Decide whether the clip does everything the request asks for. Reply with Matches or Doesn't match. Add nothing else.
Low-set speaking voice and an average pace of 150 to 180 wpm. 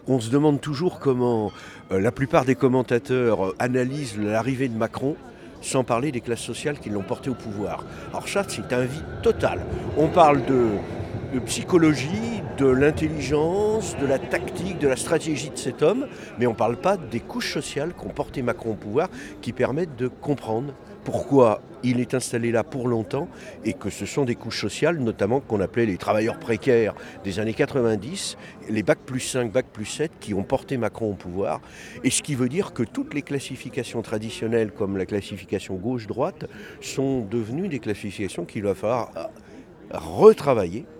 Matches